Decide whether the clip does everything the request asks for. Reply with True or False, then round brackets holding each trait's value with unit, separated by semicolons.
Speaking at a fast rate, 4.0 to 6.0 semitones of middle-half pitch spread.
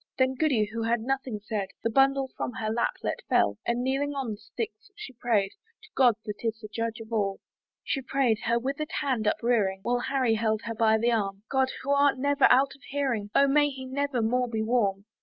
False (215 wpm; 3.6 semitones)